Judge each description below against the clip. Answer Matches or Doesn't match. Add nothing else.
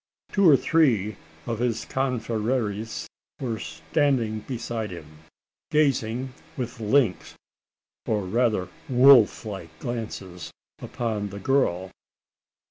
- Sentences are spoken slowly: Matches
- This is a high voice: Doesn't match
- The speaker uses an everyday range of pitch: Matches